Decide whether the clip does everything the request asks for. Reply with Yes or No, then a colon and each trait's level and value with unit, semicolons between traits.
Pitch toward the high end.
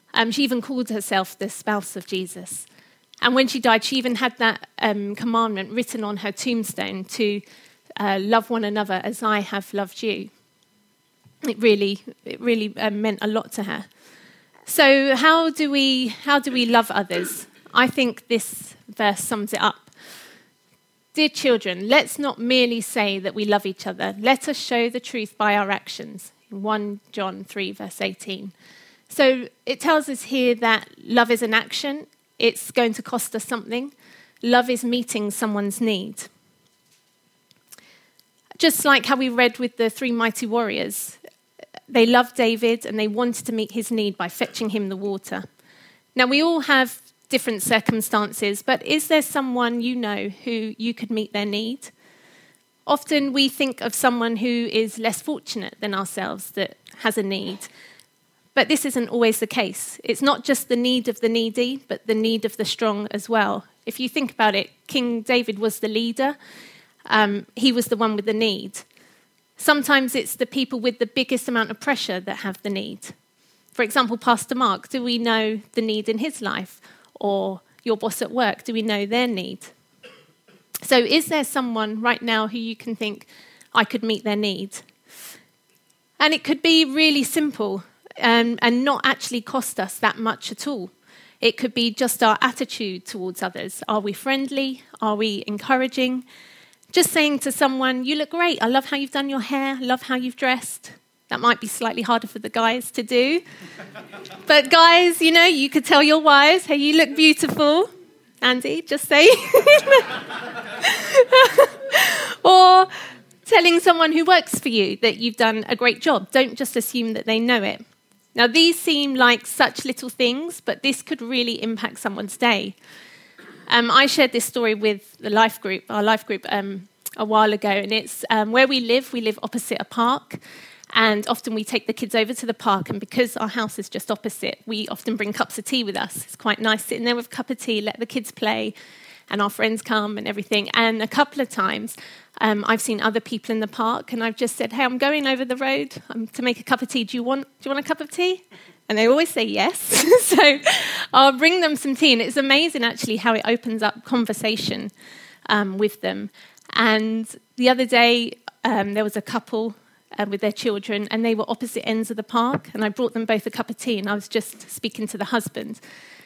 Yes: high, 235 Hz